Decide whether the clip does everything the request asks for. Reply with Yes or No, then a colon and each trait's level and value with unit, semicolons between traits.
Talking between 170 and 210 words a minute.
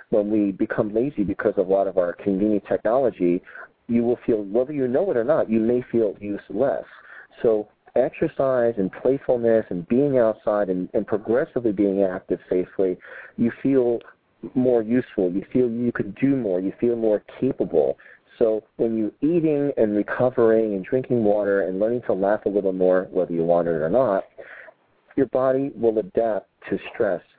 Yes: average, 175 wpm